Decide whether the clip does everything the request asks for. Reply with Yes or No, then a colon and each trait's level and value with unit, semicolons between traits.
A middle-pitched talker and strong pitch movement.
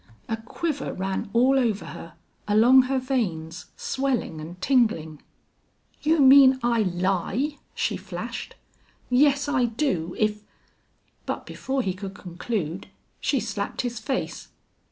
No: high, 230 Hz; wide, 6.0 semitones